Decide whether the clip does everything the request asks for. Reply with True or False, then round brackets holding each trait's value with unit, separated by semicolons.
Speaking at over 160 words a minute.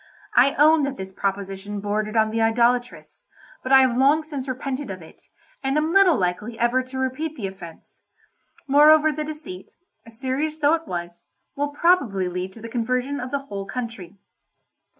True (170 wpm)